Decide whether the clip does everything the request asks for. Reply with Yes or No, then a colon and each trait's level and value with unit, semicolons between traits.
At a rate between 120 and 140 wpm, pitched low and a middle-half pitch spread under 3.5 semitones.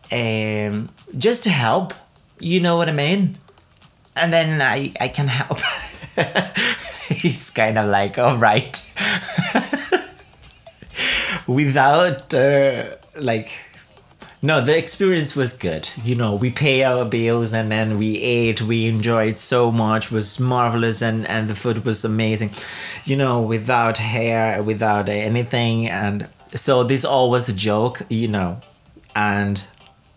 No: slow, 135 wpm; low, 120 Hz; average, 4.0 semitones